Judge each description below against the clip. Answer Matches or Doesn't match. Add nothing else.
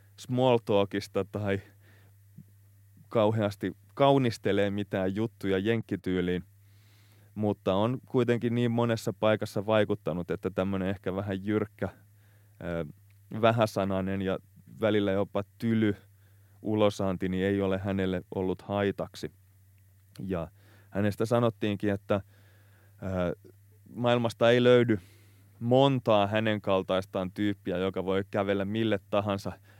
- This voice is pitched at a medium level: Doesn't match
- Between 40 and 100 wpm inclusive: Matches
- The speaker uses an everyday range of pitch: Doesn't match